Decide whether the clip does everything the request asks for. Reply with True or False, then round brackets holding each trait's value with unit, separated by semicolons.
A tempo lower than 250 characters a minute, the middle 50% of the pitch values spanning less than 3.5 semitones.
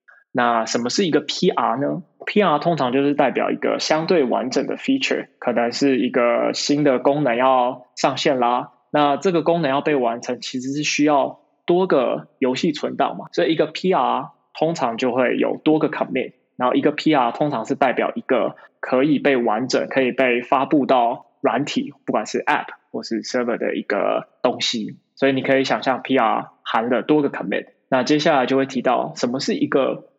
False (320 characters per minute; 2.9 semitones)